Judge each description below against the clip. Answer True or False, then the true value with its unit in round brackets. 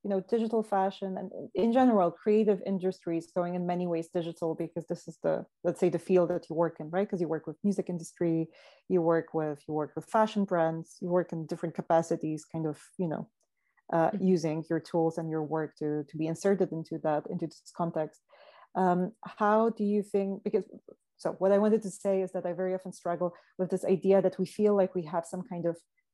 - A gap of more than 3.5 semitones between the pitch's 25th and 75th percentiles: False (2.9 semitones)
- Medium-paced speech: False (220 wpm)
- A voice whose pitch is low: False (180 Hz)